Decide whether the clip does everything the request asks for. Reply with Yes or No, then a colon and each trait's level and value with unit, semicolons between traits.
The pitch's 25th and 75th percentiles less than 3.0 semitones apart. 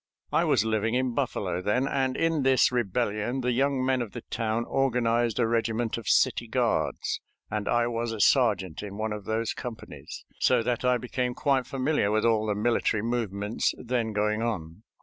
Yes: narrow, 2.6 semitones